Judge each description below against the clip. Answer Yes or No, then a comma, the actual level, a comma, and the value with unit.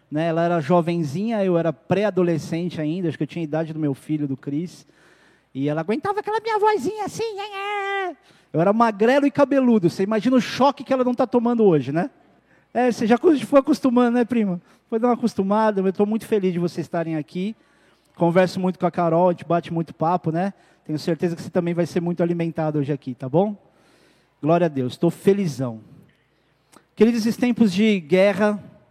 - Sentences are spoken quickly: Yes, fast, 195 wpm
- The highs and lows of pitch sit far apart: Yes, wide, 6.0 semitones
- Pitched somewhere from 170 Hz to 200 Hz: Yes, medium, 185 Hz